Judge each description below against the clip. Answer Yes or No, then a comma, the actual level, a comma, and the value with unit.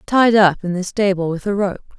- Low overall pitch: No, high, 195 Hz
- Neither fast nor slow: No, fast, 240 wpm